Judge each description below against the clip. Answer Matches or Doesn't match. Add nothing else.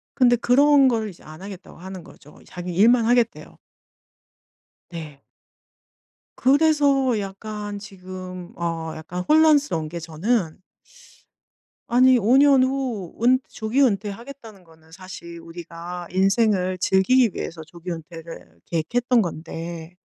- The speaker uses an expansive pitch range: Matches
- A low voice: Doesn't match